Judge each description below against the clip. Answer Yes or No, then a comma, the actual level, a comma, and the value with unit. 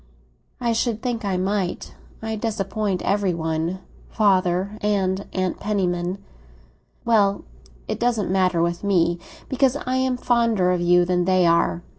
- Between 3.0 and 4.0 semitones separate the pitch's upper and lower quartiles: Yes, average, 3.7 semitones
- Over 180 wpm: No, slow, 135 wpm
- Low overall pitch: No, high, 195 Hz